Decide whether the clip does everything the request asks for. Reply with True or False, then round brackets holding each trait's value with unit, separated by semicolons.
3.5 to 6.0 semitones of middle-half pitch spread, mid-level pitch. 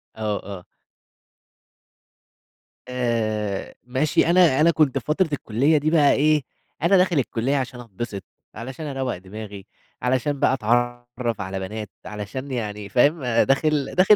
False (5.1 semitones; 125 Hz)